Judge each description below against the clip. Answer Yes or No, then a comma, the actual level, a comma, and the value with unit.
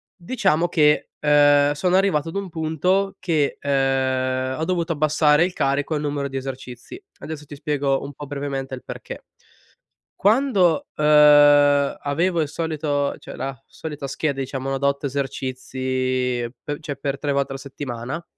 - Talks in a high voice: No, medium, 145 Hz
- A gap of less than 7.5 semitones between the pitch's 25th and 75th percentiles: Yes, average, 2.7 semitones